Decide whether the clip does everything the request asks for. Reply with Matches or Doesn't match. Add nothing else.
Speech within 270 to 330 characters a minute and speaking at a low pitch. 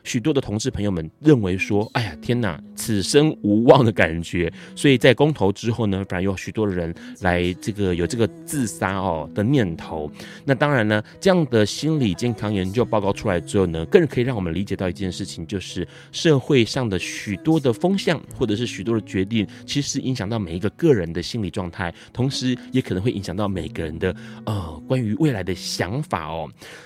Matches